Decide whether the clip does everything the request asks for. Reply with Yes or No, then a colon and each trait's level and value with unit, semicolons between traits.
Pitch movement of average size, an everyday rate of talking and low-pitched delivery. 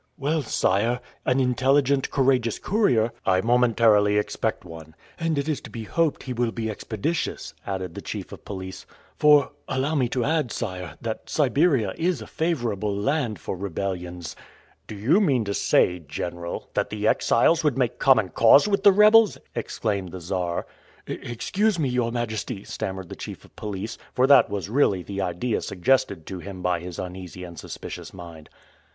No: wide, 6.5 semitones; average, 170 wpm; low, 115 Hz